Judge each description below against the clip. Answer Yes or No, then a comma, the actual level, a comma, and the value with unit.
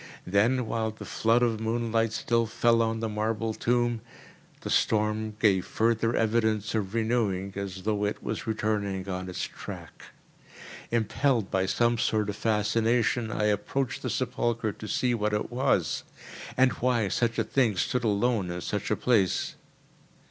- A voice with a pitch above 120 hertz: No, low, 110 Hz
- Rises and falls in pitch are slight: Yes, narrow, 2.1 semitones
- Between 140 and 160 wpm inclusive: Yes, average, 155 wpm